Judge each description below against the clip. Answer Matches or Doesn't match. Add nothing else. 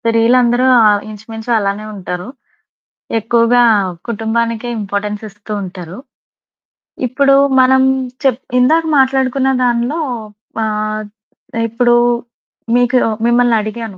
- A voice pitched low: Doesn't match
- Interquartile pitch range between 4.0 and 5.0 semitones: Doesn't match